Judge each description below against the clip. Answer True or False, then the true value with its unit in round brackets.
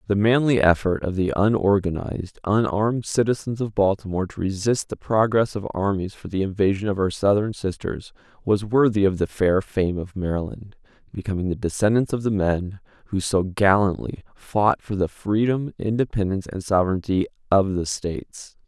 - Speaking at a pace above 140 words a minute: True (160 wpm)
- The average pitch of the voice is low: True (100 Hz)